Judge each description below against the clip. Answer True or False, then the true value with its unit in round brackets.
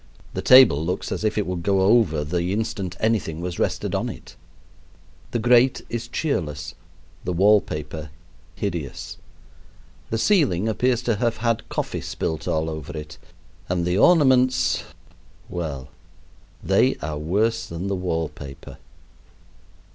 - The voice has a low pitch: True (95 Hz)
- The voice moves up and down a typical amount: False (6.1 semitones)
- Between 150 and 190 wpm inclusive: False (135 wpm)